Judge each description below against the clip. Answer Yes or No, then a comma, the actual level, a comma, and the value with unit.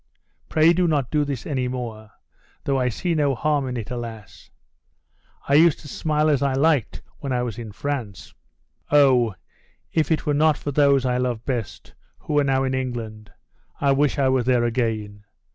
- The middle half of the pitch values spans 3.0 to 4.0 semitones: Yes, average, 3.6 semitones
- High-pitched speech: No, low, 130 Hz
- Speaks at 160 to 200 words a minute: Yes, average, 185 wpm